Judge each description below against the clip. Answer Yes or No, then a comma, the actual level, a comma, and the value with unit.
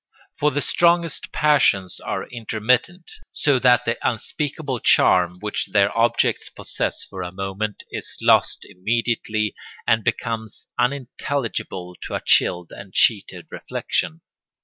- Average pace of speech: No, slow, 125 wpm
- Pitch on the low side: Yes, low, 115 Hz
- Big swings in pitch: No, average, 4.9 semitones